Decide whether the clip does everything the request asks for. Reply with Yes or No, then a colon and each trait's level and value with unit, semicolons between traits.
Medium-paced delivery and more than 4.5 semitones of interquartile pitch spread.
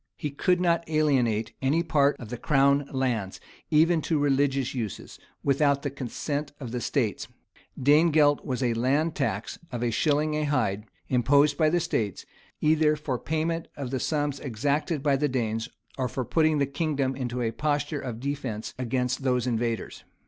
No: average, 170 wpm; average, 3.4 semitones